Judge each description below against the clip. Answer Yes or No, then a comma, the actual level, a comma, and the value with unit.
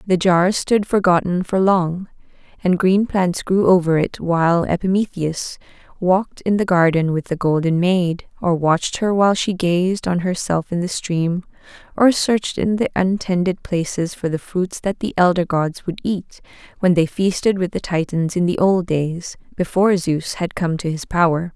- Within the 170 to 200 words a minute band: Yes, average, 180 wpm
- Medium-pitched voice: Yes, medium, 180 Hz